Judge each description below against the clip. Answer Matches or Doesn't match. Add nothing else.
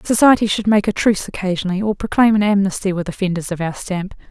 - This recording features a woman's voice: Matches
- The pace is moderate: Doesn't match